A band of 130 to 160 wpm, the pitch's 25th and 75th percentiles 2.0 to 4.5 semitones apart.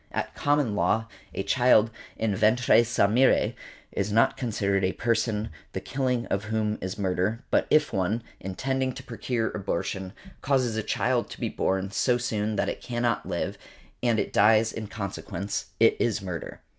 No: average, 170 wpm; average, 3.3 semitones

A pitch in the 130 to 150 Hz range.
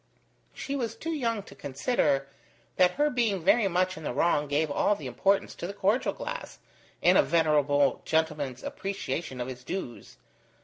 No: medium, 170 Hz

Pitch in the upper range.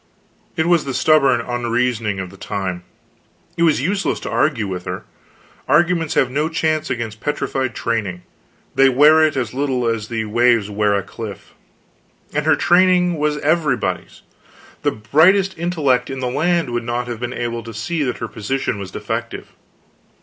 No: low, 125 Hz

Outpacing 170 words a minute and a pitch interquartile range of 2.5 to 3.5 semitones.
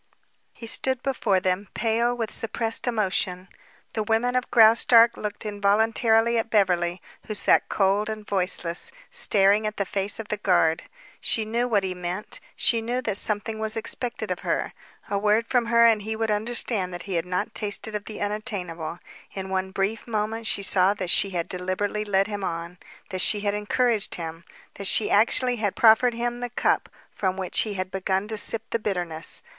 Yes: average, 185 wpm; average, 3.0 semitones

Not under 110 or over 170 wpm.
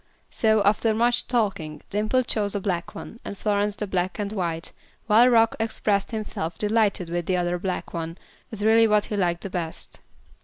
No: average, 185 wpm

